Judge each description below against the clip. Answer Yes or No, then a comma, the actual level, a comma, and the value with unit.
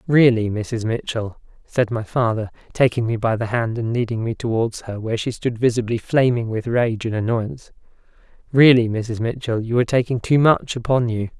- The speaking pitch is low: Yes, low, 115 Hz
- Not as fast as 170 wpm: No, average, 185 wpm